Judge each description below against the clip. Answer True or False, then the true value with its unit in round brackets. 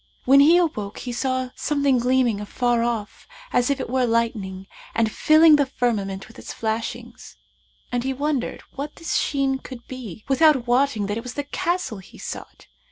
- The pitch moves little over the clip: False (3.6 semitones)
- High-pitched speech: True (250 Hz)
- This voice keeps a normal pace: True (175 wpm)